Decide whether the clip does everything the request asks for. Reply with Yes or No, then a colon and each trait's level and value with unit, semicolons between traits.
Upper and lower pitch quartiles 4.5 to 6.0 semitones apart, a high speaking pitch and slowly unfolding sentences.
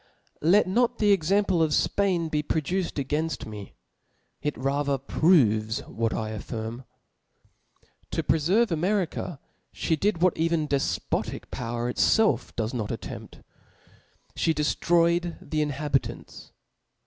No: average, 5.0 semitones; medium, 155 Hz; slow, 125 wpm